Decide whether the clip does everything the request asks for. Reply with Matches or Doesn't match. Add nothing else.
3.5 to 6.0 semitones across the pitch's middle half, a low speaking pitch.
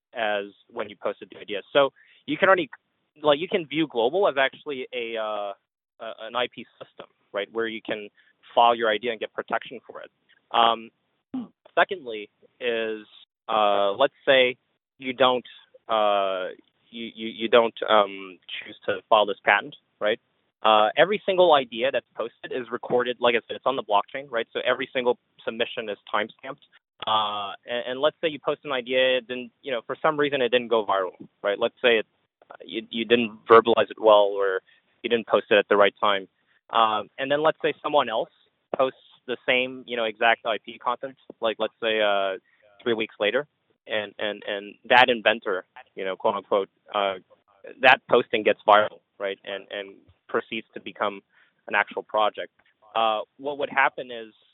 Matches